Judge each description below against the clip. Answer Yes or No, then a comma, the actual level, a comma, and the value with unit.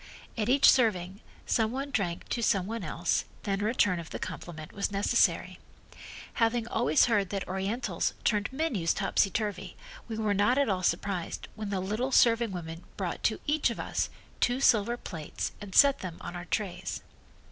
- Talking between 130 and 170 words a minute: No, average, 180 wpm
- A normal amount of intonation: Yes, average, 4.2 semitones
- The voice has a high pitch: Yes, high, 205 Hz